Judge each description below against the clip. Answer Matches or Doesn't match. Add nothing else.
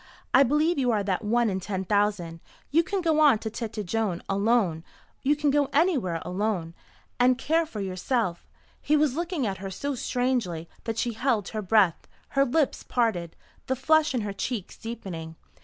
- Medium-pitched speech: Doesn't match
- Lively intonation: Matches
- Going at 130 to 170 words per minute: Doesn't match